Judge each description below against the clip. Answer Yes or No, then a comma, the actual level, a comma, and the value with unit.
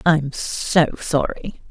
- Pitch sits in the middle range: Yes, medium, 155 Hz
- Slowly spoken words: Yes, slow, 105 wpm